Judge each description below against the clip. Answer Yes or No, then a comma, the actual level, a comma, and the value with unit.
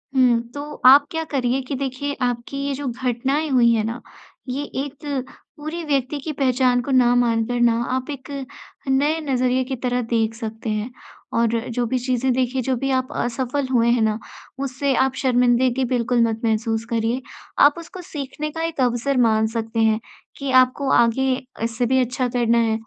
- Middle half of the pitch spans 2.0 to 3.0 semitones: Yes, narrow, 2.5 semitones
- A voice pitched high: Yes, very high, 250 Hz